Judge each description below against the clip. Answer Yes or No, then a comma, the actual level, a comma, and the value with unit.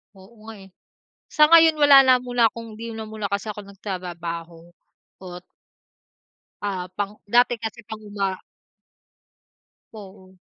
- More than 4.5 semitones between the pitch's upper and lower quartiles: No, average, 3.6 semitones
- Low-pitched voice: No, high, 210 Hz